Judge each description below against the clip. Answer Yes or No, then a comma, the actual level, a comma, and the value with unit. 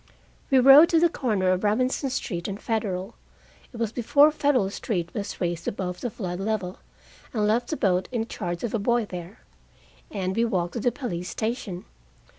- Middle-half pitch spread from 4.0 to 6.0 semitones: Yes, average, 4.9 semitones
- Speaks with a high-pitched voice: Yes, high, 215 Hz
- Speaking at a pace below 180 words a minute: No, average, 185 wpm